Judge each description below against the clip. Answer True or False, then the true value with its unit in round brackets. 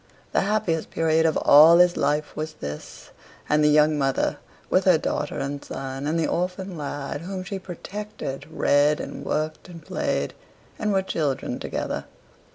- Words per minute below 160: False (165 wpm)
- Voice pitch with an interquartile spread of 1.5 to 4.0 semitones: True (3.7 semitones)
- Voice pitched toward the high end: False (155 Hz)